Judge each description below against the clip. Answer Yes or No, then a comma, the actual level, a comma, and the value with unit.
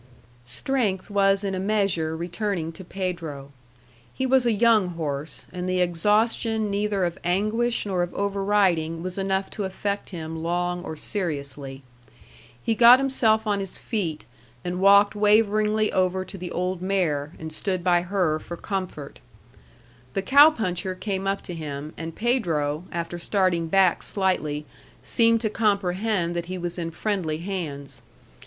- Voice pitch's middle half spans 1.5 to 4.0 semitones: Yes, average, 3.6 semitones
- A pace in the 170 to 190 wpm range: No, average, 155 wpm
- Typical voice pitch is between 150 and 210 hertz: Yes, medium, 185 Hz